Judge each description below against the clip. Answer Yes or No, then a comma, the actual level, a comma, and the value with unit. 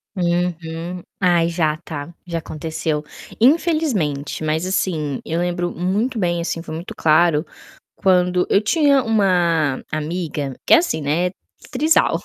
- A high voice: No, medium, 175 Hz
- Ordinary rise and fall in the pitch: Yes, average, 3.1 semitones